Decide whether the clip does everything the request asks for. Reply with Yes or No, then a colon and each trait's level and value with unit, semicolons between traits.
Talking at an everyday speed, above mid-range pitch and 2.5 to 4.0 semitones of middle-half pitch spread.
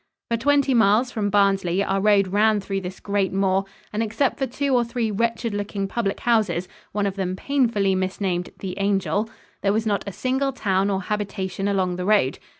Yes: average, 190 wpm; high, 200 Hz; average, 2.8 semitones